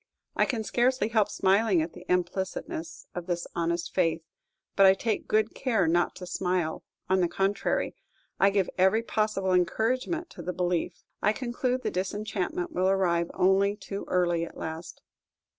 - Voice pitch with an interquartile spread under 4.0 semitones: Yes, average, 3.4 semitones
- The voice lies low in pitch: No, high, 190 Hz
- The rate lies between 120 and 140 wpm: No, average, 160 wpm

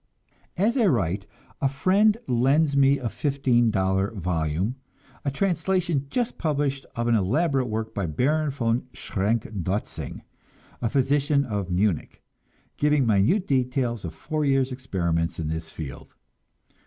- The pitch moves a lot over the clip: Yes, wide, 6.4 semitones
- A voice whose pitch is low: Yes, low, 125 Hz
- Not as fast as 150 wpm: Yes, slow, 135 wpm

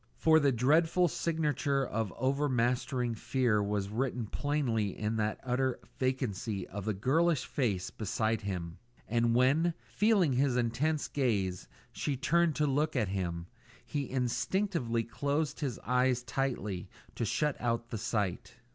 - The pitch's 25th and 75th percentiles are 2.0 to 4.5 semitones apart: No, average, 4.9 semitones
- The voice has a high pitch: No, low, 125 Hz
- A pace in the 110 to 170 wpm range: Yes, average, 140 wpm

